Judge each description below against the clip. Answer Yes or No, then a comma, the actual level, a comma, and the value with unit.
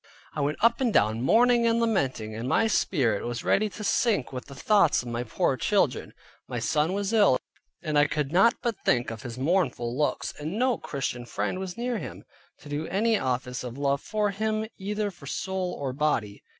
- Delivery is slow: No, average, 200 wpm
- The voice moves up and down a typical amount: No, wide, 8.8 semitones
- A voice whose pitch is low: No, medium, 155 Hz